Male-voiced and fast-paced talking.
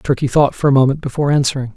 Yes: male; fast, 240 wpm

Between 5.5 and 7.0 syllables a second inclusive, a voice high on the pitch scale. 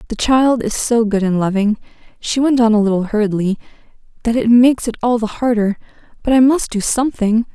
Yes: 5.8 syllables/s; high, 225 Hz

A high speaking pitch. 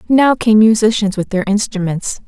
Yes: high, 210 Hz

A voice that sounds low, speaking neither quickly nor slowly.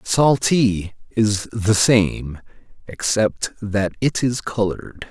No: low, 105 Hz; slow, 105 wpm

